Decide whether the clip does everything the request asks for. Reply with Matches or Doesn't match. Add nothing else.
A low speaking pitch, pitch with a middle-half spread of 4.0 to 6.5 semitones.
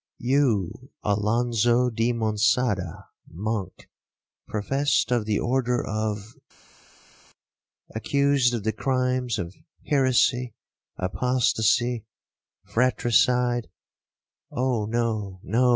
Doesn't match